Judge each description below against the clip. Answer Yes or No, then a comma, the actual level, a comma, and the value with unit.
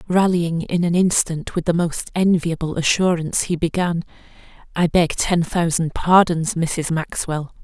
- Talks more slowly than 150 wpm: Yes, slow, 135 wpm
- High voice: No, medium, 170 Hz